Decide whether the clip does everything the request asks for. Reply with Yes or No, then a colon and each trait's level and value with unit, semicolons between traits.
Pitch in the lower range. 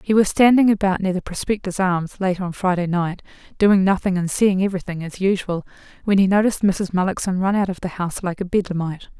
No: high, 190 Hz